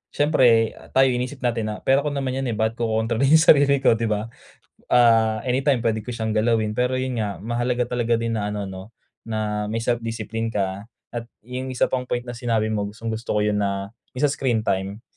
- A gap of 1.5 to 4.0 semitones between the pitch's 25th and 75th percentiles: Yes, narrow, 2.6 semitones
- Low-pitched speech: Yes, low, 115 Hz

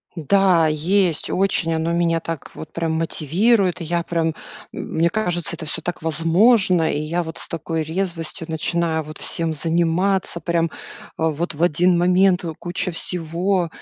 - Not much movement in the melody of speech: Yes, narrow, 1.9 semitones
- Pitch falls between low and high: Yes, medium, 170 Hz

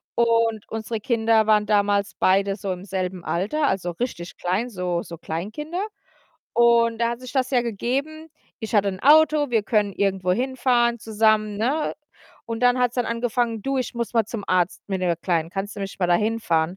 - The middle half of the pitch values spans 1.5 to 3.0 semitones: No, average, 3.8 semitones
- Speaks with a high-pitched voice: Yes, high, 220 Hz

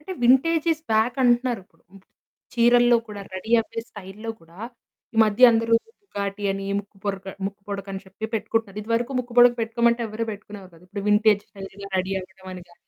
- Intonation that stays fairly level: No, average, 3.3 semitones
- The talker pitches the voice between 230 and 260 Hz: No, high, 215 Hz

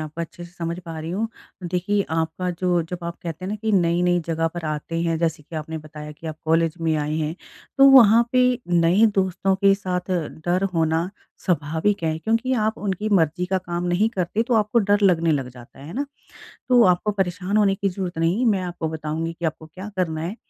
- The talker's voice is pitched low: No, medium, 175 Hz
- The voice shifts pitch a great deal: No, average, 3.3 semitones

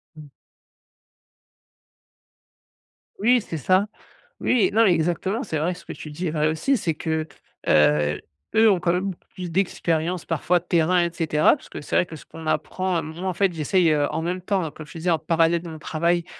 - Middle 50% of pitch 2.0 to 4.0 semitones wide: Yes, average, 2.7 semitones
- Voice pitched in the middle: Yes, medium, 170 Hz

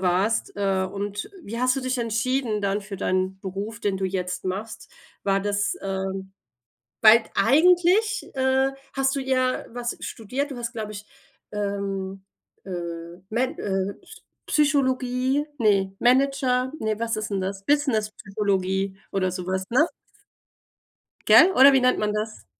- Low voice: No, high, 215 Hz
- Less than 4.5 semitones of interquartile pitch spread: No, average, 4.8 semitones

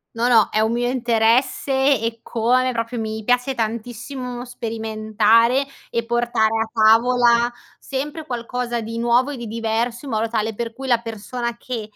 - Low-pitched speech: No, high, 235 Hz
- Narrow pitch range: Yes, narrow, 1.7 semitones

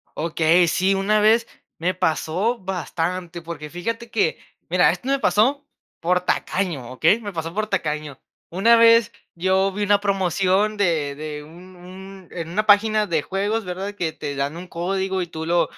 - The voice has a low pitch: No, medium, 185 Hz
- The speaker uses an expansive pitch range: No, average, 3.7 semitones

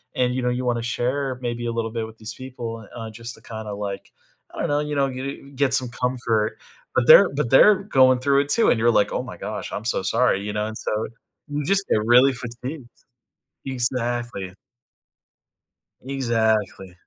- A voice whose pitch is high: No, low, 120 Hz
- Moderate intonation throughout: Yes, average, 3.0 semitones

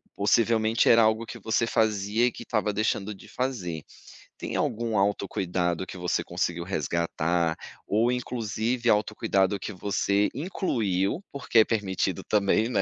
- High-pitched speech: No, low, 105 Hz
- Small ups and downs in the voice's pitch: No, average, 3.3 semitones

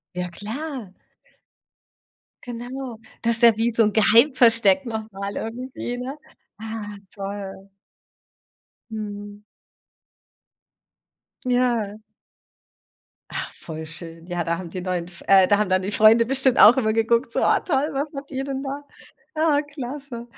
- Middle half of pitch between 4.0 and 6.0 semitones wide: Yes, average, 4.6 semitones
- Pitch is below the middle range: No, high, 225 Hz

